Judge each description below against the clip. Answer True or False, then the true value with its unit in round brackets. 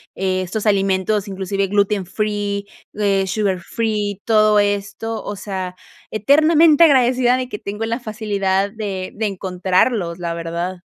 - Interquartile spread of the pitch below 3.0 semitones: True (2.5 semitones)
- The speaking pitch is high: True (205 Hz)